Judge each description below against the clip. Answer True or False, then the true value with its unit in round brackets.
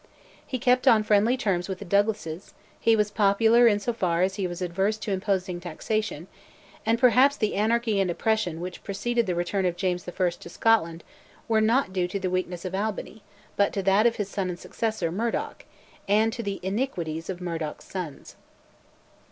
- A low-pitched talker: False (200 Hz)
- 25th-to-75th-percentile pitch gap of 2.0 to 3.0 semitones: False (3.6 semitones)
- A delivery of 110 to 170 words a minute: False (185 wpm)